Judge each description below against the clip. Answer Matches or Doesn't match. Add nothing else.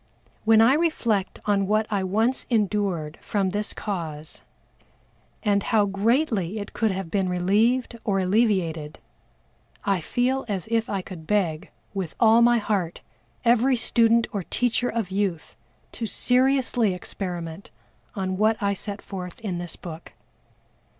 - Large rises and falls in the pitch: Doesn't match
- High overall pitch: Matches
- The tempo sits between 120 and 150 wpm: Matches